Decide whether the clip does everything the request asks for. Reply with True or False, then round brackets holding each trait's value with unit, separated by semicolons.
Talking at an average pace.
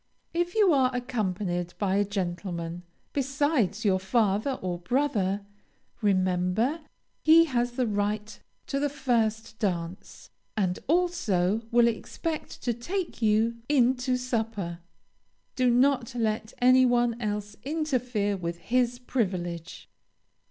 False (120 wpm)